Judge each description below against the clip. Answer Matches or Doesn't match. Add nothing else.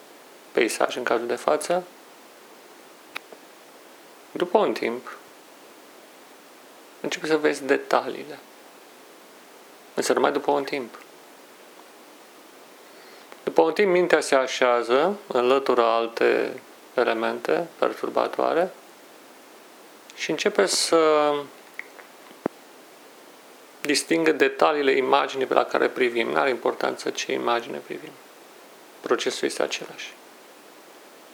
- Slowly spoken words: Matches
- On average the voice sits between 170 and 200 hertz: Doesn't match